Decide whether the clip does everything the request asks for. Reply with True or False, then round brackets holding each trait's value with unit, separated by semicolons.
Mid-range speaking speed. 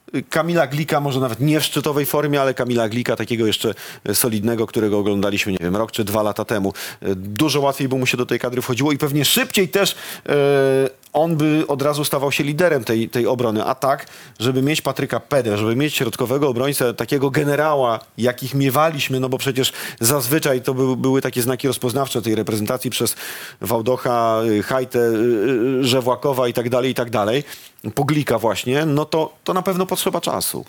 False (170 wpm)